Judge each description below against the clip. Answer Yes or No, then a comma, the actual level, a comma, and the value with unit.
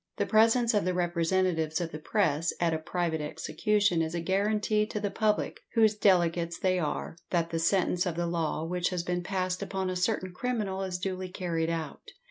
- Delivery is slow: No, average, 195 wpm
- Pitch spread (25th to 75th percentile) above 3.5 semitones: No, average, 3.0 semitones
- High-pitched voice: No, medium, 180 Hz